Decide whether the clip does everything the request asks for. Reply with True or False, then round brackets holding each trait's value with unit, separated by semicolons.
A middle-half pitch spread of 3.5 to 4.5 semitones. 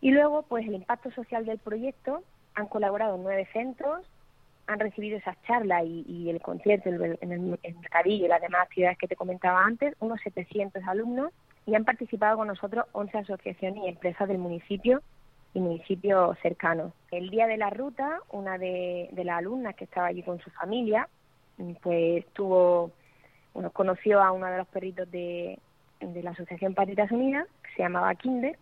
True (3.9 semitones)